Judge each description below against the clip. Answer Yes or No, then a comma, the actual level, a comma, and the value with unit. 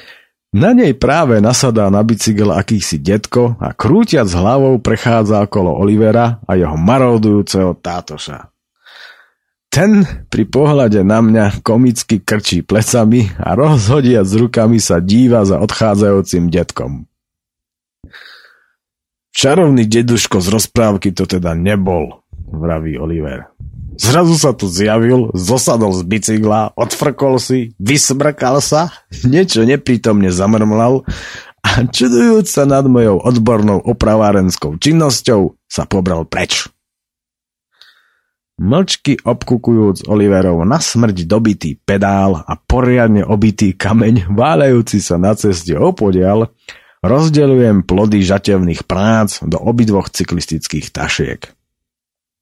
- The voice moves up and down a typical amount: Yes, average, 4.0 semitones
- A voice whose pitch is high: No, low, 110 Hz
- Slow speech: Yes, slow, 105 wpm